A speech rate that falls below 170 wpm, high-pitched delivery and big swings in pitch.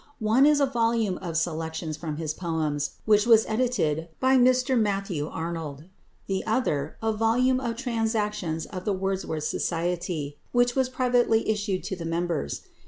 Yes: average, 155 wpm; high, 195 Hz; wide, 6.2 semitones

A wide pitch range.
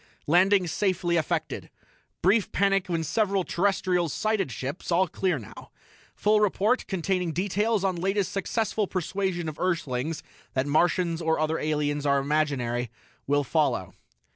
No: average, 4.3 semitones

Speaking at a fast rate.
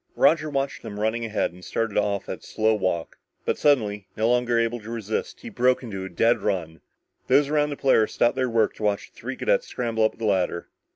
Yes: fast, 225 wpm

